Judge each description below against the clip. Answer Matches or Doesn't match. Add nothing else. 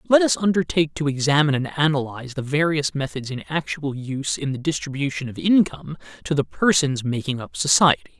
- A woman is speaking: Doesn't match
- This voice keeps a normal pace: Matches